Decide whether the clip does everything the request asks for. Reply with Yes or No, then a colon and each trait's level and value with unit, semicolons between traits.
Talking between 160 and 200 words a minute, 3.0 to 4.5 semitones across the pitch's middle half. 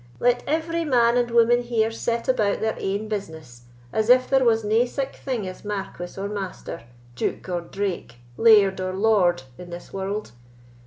Yes: average, 170 wpm; average, 3.9 semitones